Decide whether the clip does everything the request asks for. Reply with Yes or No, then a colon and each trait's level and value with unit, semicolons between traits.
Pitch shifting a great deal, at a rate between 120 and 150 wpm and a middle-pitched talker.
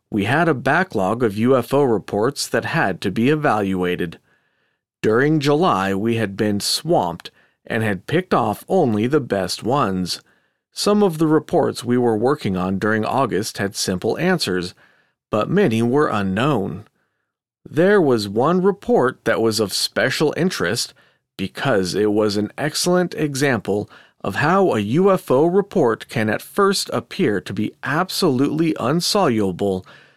No: wide, 7.2 semitones; average, 140 wpm; low, 115 Hz